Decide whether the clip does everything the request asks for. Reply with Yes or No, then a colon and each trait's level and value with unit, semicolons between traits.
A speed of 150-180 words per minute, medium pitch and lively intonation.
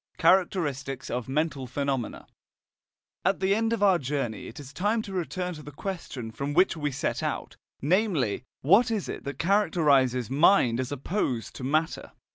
Yes: average, 165 wpm; medium, 150 Hz; wide, 6.2 semitones